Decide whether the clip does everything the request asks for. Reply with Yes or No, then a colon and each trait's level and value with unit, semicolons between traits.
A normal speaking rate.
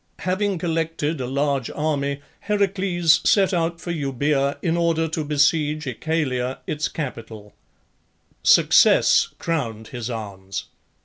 No: slow, 115 wpm